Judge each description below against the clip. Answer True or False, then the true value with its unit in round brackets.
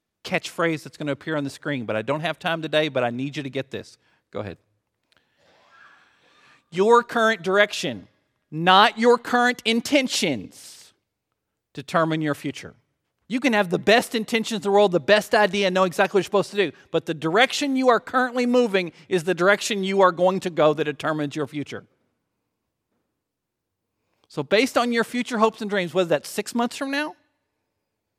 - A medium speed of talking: True (180 wpm)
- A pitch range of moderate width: False (7.0 semitones)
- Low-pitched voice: False (190 Hz)